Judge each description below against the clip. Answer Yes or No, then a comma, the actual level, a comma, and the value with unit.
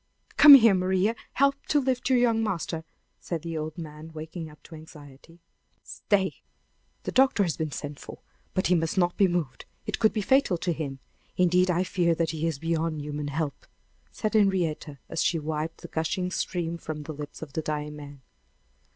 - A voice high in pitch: No, medium, 165 Hz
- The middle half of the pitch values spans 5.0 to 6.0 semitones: No, average, 3.5 semitones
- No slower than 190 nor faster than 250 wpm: Yes, average, 195 wpm